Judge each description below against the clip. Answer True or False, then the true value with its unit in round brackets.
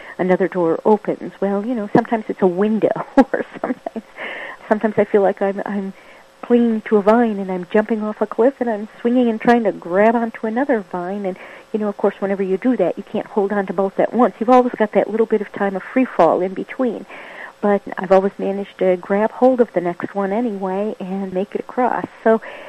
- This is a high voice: True (210 Hz)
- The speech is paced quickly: True (225 wpm)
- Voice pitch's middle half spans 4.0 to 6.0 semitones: False (3.2 semitones)